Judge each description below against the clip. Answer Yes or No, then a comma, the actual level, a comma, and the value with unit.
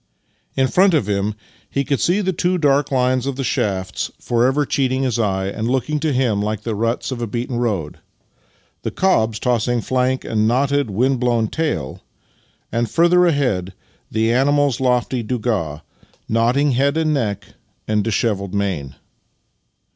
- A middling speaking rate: Yes, average, 155 wpm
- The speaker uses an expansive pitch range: No, average, 4.4 semitones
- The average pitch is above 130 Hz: No, low, 120 Hz